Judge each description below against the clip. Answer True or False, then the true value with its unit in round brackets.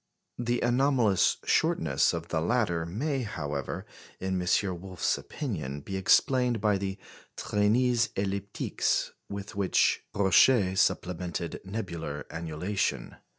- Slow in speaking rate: True (110 wpm)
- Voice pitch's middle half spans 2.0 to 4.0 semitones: False (4.7 semitones)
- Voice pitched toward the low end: True (100 Hz)